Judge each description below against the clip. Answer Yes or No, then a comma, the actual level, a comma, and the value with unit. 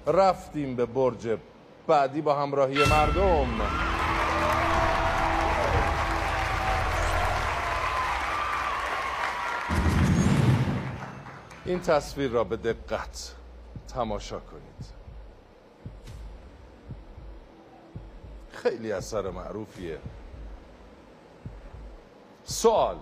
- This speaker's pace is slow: Yes, slow, 45 wpm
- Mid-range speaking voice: No, very low, 95 Hz